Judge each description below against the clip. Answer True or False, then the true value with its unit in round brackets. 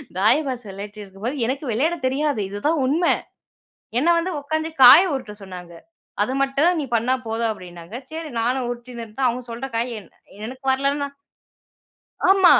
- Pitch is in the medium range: False (255 Hz)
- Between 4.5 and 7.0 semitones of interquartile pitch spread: True (4.9 semitones)